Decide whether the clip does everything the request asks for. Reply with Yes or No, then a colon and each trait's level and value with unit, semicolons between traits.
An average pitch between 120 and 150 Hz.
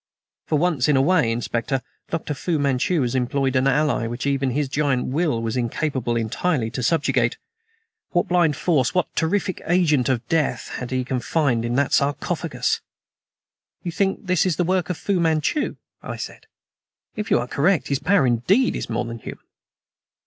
Yes: medium, 140 Hz